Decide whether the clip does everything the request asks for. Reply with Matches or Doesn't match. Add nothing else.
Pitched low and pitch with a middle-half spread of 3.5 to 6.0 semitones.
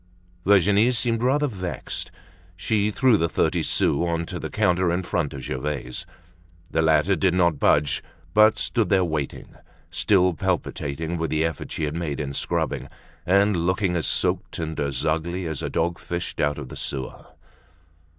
Matches